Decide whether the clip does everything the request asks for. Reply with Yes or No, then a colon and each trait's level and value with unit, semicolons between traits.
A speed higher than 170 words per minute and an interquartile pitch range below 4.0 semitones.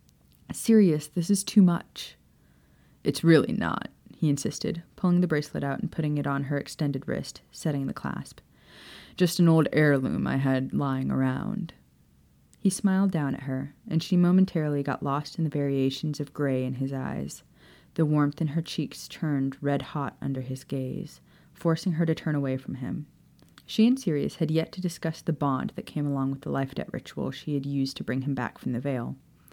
Yes: average, 190 wpm; average, 3.4 semitones